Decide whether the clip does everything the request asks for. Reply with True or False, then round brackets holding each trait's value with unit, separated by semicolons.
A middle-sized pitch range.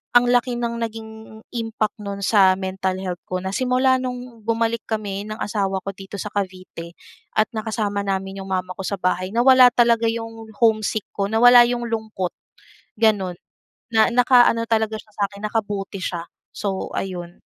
True (3.1 semitones)